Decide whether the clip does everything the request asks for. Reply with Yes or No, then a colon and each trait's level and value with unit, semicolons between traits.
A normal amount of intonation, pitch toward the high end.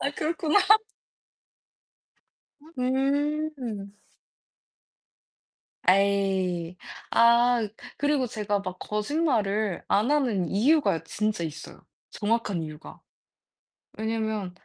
Yes: average, 4.0 semitones; high, 210 Hz